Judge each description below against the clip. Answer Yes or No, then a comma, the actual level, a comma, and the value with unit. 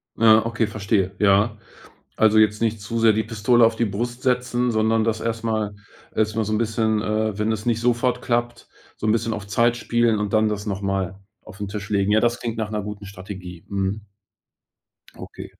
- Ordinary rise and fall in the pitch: No, narrow, 1.9 semitones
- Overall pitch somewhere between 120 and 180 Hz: No, low, 110 Hz